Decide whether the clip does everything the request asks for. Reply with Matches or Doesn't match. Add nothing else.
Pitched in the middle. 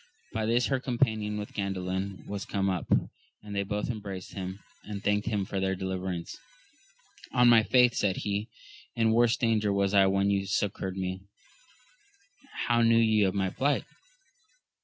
Doesn't match